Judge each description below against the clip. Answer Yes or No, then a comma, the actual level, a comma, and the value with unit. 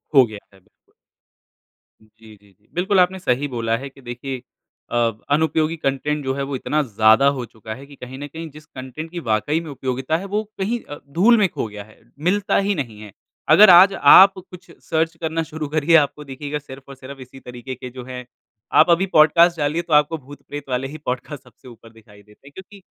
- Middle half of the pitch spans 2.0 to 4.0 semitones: No, average, 4.5 semitones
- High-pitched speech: No, medium, 140 Hz